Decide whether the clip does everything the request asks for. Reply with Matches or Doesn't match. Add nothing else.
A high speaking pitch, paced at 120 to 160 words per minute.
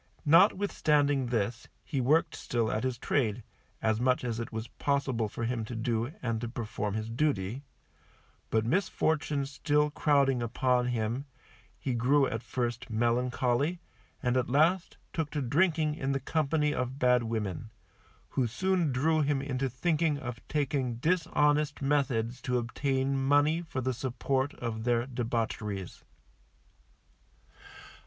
Doesn't match